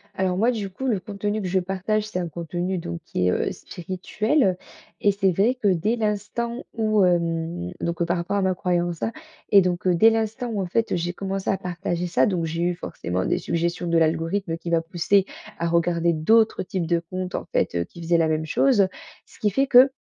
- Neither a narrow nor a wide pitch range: Yes, average, 3.4 semitones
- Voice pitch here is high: No, medium, 180 Hz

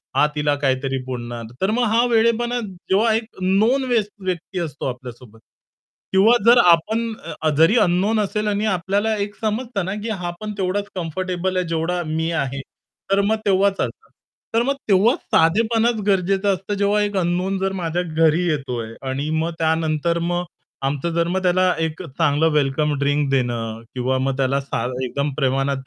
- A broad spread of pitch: Yes, wide, 5.7 semitones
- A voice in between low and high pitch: Yes, medium, 175 Hz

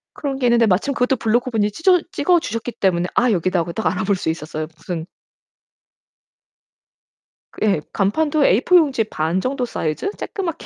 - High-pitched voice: Yes, high, 220 Hz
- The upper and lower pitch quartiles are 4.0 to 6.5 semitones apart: No, wide, 7.1 semitones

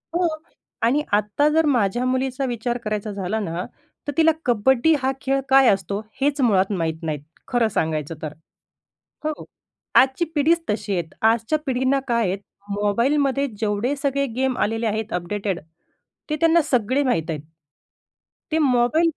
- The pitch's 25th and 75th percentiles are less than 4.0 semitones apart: No, average, 5.3 semitones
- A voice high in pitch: Yes, high, 240 Hz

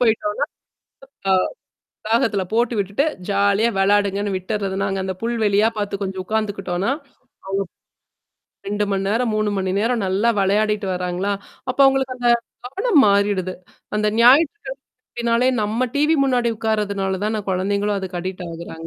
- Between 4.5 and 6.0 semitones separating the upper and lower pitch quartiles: No, average, 3.2 semitones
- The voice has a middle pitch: No, high, 205 Hz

